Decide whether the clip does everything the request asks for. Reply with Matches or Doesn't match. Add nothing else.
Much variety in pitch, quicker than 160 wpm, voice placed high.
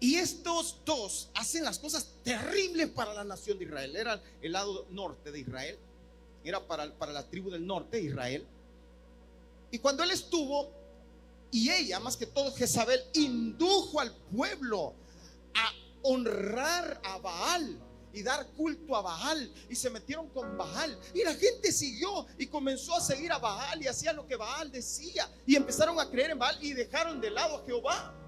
Matches